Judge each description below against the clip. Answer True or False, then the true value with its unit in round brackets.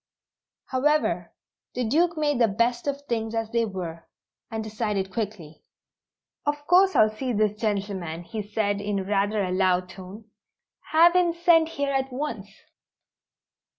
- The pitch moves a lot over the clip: True (6.1 semitones)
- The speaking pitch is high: True (220 Hz)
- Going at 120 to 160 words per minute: True (145 wpm)